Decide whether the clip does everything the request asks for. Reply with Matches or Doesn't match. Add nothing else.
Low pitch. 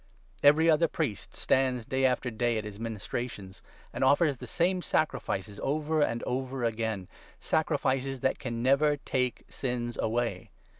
Matches